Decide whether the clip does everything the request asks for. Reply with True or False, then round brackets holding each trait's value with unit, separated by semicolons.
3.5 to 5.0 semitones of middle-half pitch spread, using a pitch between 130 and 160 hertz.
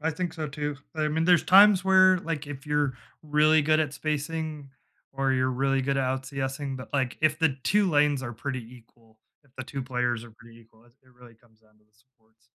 True (3.9 semitones; 135 Hz)